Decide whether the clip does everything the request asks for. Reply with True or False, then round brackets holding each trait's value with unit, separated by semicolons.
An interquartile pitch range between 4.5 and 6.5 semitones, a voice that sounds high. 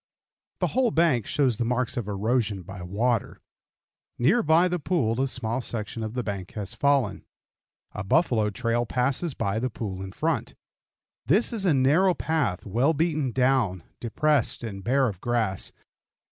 False (5.3 semitones; 120 Hz)